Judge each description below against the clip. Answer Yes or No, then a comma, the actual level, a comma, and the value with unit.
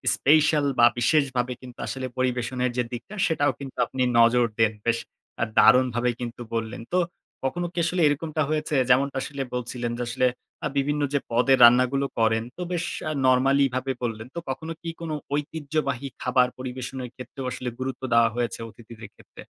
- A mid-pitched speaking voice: No, low, 130 Hz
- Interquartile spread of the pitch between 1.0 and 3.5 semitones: Yes, average, 2.8 semitones